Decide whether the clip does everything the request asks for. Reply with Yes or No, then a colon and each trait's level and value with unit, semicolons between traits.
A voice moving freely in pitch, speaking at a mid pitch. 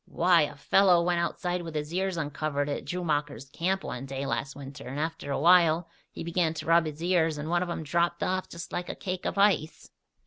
No: average, 3.1 semitones; medium, 165 Hz